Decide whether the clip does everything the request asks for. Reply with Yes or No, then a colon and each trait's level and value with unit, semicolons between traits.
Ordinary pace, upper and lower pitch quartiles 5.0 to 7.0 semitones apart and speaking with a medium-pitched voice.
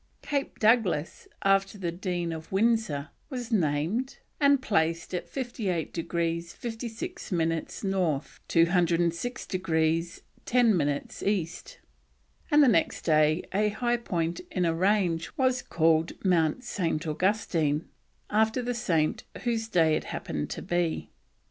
No: slow, 130 wpm; wide, 5.4 semitones; medium, 180 Hz